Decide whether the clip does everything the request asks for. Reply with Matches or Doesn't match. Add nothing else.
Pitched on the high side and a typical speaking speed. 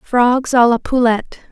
Matches